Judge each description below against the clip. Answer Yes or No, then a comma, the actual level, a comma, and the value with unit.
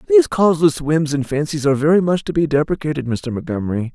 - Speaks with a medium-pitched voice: Yes, medium, 145 Hz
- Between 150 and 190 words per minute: No, average, 200 wpm